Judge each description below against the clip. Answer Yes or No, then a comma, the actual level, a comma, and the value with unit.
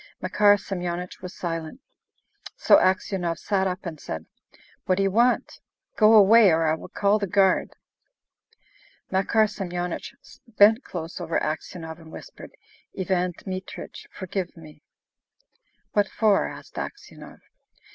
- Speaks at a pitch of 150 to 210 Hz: Yes, medium, 185 Hz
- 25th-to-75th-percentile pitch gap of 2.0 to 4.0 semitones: Yes, average, 2.9 semitones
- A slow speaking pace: Yes, slow, 125 wpm